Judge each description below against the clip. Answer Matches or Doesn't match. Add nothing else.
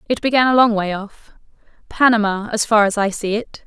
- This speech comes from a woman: Matches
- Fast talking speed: Doesn't match